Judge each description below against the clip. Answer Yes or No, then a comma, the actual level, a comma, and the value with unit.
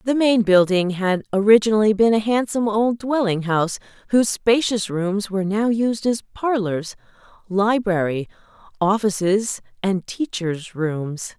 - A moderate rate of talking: No, slow, 125 wpm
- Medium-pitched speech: No, high, 205 Hz